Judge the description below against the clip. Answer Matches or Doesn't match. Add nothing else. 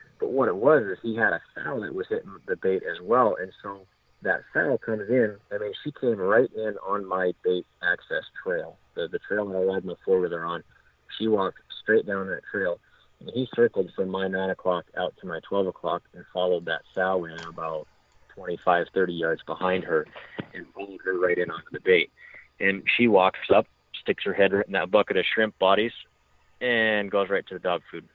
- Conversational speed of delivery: Doesn't match